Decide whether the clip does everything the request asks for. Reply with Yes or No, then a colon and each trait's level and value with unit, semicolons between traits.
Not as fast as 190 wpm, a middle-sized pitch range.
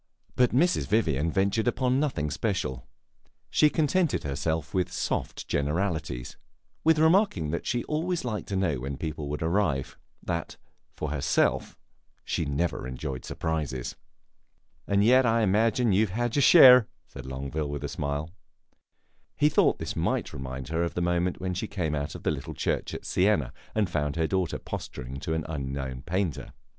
No: average, 165 wpm; wide, 7.7 semitones